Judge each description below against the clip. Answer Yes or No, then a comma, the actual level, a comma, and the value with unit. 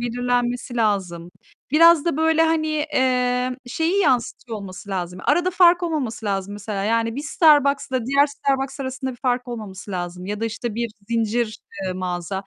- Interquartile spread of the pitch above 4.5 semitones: Yes, average, 5.3 semitones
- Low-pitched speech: No, high, 245 Hz